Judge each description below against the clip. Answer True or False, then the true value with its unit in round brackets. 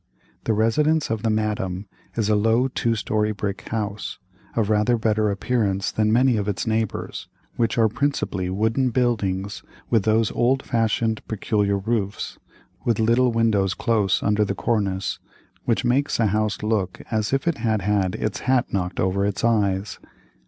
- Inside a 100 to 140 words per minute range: False (160 wpm)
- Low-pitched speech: True (110 Hz)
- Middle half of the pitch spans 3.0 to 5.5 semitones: False (2.5 semitones)